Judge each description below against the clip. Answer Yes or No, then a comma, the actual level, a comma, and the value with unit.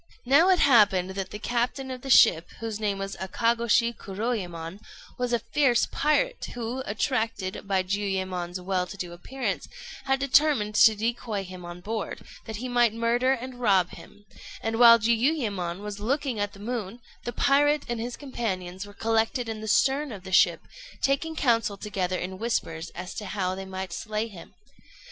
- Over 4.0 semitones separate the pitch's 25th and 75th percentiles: Yes, average, 4.4 semitones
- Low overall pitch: No, high, 220 Hz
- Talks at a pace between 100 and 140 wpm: No, average, 175 wpm